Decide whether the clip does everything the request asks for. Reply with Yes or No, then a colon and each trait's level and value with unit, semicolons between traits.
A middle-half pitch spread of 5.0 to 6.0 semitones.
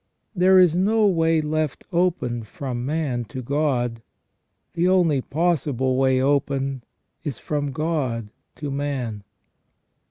No: average, 4.1 semitones